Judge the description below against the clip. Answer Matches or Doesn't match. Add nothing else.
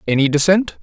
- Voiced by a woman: Doesn't match